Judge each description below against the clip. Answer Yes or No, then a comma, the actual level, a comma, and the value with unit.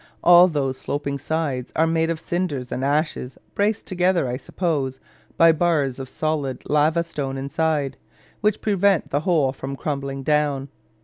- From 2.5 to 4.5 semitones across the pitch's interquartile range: Yes, average, 3.6 semitones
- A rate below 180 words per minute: Yes, average, 150 wpm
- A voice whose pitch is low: No, medium, 150 Hz